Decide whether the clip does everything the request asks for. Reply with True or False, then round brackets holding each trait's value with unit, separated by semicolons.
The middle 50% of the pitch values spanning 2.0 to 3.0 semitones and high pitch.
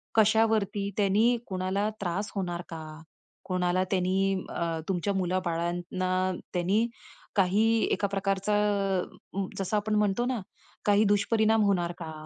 True (2.5 semitones; 195 Hz)